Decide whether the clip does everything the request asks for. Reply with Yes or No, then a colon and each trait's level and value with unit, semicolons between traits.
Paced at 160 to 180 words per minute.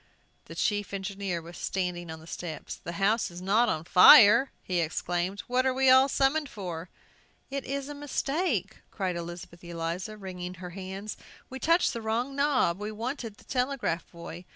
Yes: average, 170 wpm